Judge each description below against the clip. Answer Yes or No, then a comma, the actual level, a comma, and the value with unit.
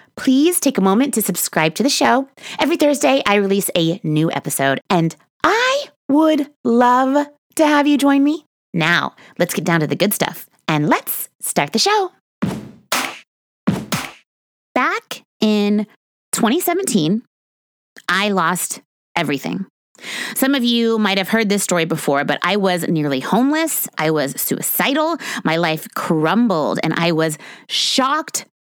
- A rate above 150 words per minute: No, average, 145 wpm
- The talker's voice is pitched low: No, high, 225 Hz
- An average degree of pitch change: No, wide, 8.9 semitones